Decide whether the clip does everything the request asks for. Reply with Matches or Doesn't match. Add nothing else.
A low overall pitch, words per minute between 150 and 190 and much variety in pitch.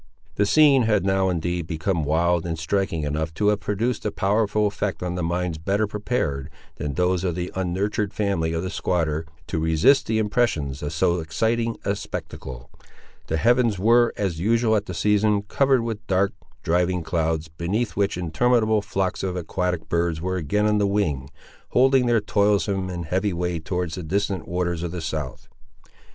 Doesn't match